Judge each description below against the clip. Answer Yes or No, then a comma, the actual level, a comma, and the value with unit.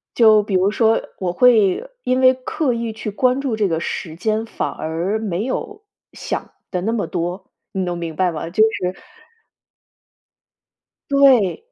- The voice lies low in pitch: No, high, 215 Hz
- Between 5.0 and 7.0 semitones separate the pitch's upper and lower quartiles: Yes, wide, 5.4 semitones